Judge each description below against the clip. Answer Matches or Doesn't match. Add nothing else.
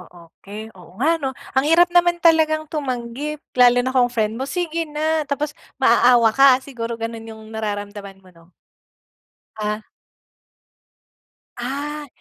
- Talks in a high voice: Matches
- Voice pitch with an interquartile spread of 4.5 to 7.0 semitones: Matches